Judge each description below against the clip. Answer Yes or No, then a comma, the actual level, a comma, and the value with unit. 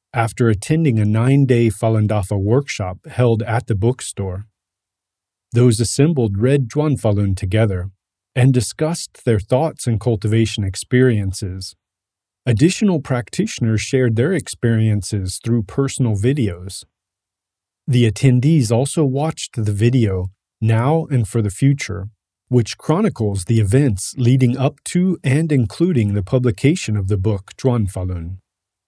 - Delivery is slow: Yes, slow, 125 wpm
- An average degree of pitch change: Yes, average, 4.4 semitones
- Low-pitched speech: Yes, low, 115 Hz